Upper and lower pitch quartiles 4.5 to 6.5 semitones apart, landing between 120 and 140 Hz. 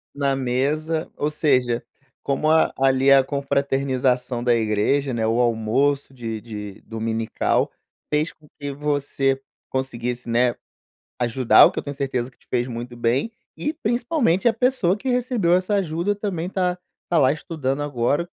Yes: average, 4.8 semitones; low, 135 Hz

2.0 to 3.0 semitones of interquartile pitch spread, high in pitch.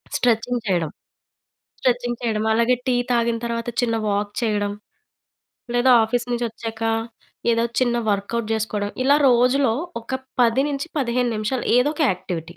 Yes: narrow, 2.4 semitones; high, 235 Hz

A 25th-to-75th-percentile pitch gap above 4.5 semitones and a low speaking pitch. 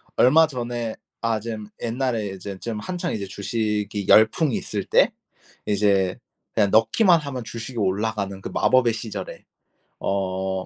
No: average, 3.3 semitones; low, 110 Hz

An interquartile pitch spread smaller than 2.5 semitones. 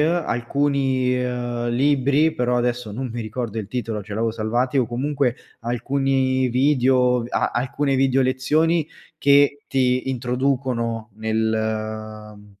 No: average, 2.8 semitones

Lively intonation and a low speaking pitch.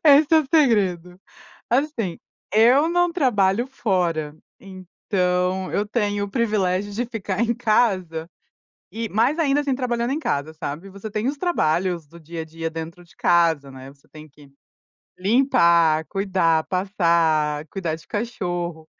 No: wide, 6.0 semitones; high, 190 Hz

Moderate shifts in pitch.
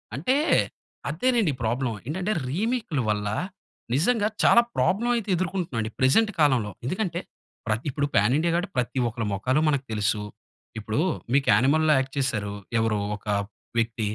No: wide, 8.1 semitones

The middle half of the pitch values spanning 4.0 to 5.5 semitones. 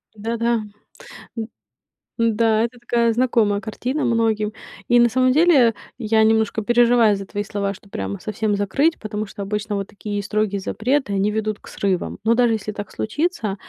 No: narrow, 2.5 semitones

